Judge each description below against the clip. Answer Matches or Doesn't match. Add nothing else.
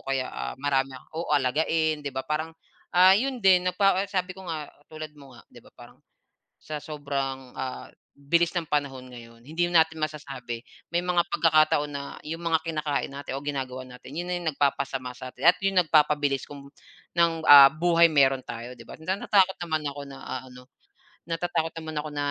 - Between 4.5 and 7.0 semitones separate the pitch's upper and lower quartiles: Doesn't match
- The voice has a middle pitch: Matches